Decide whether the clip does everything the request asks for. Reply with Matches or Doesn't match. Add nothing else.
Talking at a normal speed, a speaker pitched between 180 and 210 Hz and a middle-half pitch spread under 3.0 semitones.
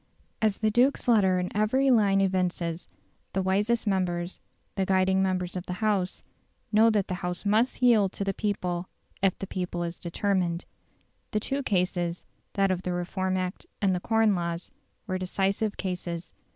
Matches